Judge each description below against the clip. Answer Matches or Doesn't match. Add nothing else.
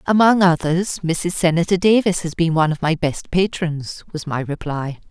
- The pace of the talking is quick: Doesn't match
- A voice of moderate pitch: Matches